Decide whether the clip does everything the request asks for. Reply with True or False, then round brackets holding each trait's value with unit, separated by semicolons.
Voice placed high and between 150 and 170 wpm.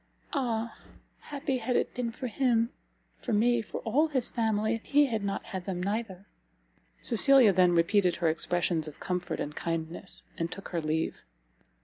True (215 Hz; 165 wpm)